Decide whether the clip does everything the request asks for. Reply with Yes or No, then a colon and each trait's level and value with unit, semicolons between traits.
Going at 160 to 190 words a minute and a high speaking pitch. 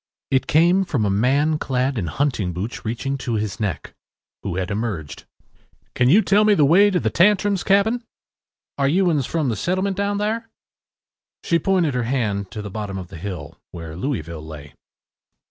No: average, 185 wpm; low, 130 Hz